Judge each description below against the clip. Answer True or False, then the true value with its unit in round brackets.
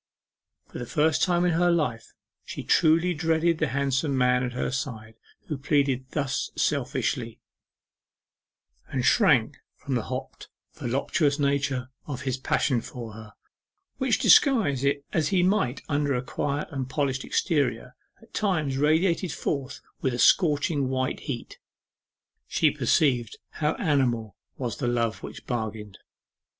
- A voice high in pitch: False (140 Hz)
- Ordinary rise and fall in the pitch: True (3.7 semitones)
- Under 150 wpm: True (140 wpm)